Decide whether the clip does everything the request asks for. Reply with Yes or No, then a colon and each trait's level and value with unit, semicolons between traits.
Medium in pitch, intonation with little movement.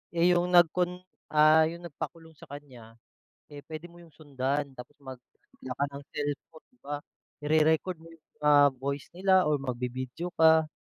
No: medium, 155 Hz; average, 3.1 semitones